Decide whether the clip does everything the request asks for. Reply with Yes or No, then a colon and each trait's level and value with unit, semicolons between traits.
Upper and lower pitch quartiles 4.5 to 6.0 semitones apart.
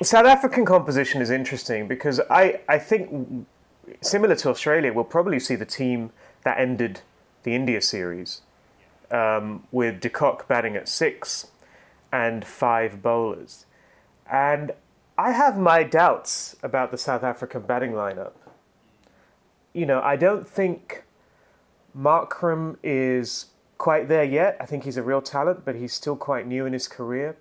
Yes: average, 4.8 semitones